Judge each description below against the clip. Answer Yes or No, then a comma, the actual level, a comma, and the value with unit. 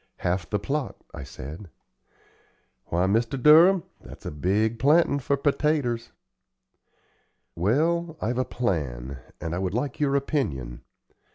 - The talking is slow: Yes, slow, 120 wpm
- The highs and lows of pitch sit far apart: Yes, wide, 8.5 semitones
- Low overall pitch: Yes, low, 120 Hz